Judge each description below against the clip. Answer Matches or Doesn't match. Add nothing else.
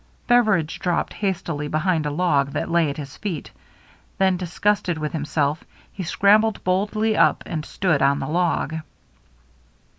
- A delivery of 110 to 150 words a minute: Matches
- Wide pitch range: Doesn't match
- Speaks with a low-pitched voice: Doesn't match